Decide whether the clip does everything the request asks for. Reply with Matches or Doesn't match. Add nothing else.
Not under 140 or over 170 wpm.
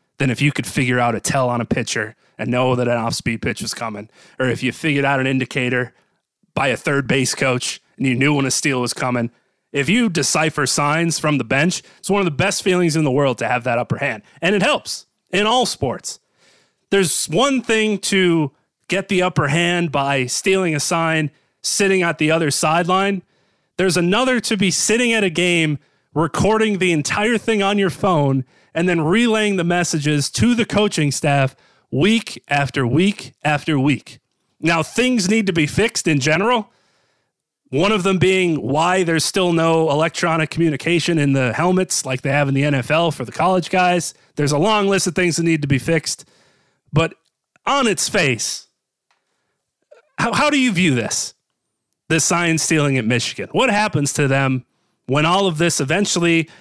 Doesn't match